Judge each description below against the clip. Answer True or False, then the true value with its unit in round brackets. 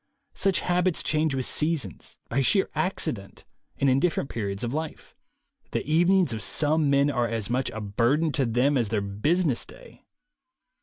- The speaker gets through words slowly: False (165 wpm)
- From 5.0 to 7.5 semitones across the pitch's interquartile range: True (5.6 semitones)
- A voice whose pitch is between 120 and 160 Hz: True (140 Hz)